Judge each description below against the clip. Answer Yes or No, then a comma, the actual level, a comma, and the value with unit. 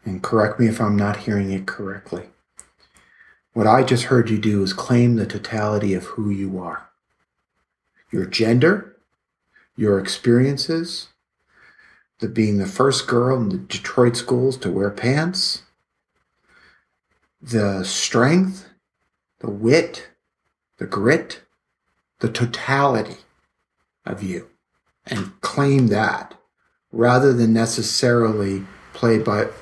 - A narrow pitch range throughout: No, average, 3.6 semitones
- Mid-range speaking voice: No, low, 115 Hz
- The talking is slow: Yes, slow, 115 wpm